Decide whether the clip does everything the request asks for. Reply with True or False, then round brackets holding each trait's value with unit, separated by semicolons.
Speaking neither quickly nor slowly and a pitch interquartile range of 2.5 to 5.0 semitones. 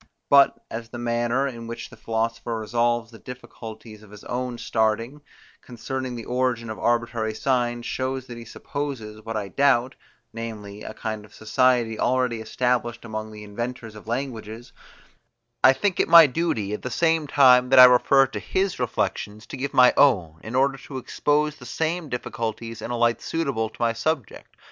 True (175 wpm; 2.8 semitones)